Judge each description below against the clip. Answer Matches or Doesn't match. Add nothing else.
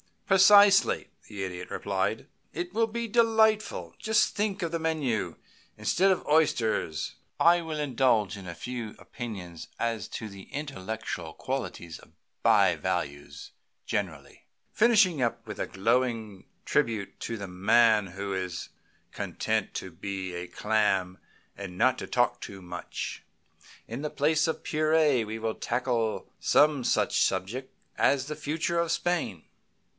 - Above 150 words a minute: Doesn't match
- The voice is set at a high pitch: Doesn't match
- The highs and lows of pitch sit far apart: Matches